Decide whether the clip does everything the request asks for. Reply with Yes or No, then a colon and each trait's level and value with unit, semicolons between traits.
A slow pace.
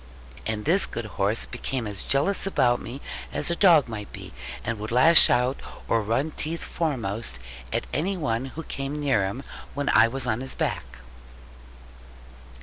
No: average, 165 wpm